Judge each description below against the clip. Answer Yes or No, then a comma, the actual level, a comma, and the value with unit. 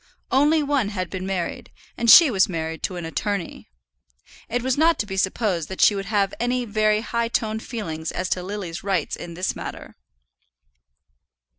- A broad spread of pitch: No, average, 4.2 semitones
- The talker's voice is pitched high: Yes, high, 205 Hz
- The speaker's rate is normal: Yes, average, 175 wpm